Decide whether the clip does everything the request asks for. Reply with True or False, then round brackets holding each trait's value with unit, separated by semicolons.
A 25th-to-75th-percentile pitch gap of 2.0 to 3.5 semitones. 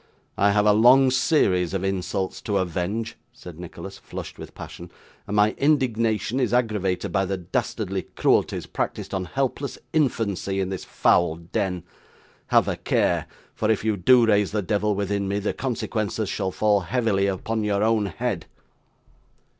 True (3.0 semitones)